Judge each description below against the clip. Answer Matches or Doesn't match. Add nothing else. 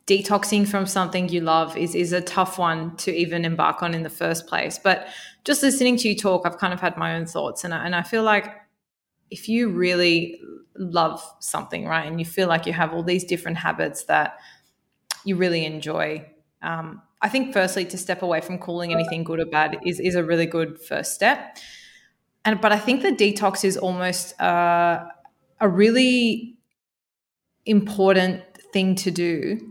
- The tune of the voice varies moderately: Matches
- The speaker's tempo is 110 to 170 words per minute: Doesn't match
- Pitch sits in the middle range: Matches